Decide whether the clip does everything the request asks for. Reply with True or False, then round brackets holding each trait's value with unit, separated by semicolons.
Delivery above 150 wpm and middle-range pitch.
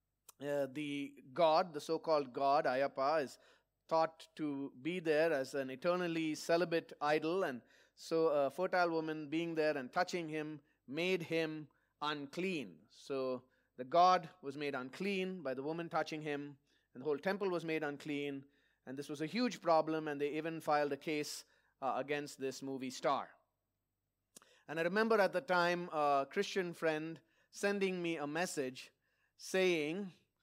True (160 wpm; 155 Hz)